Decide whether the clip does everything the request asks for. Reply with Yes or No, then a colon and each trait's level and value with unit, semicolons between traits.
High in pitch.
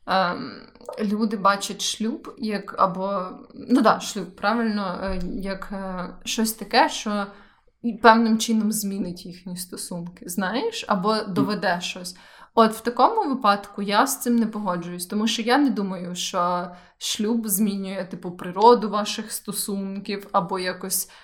Yes: high, 205 Hz